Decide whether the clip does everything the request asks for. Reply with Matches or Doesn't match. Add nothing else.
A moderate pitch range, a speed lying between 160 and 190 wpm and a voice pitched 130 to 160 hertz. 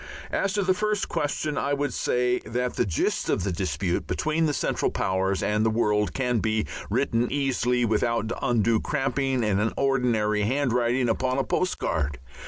Doesn't match